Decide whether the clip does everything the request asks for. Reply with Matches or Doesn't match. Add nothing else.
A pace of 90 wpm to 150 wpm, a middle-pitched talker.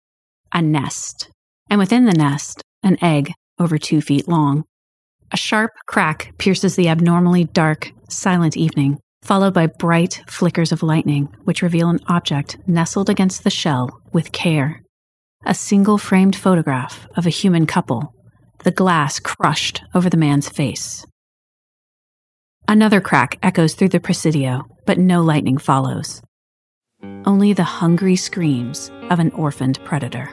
Matches